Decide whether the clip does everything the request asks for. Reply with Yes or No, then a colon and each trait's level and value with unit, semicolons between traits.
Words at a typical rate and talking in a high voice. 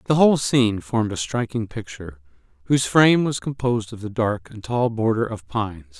No: average, 190 wpm; low, 115 Hz